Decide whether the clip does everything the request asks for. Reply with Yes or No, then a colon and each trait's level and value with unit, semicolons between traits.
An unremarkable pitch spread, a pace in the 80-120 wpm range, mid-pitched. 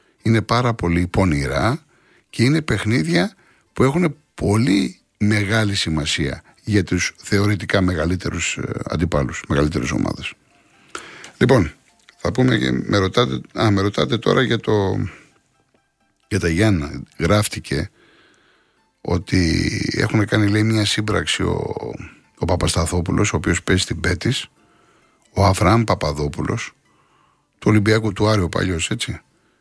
No: average, 4.1 semitones; slow, 115 wpm; low, 100 Hz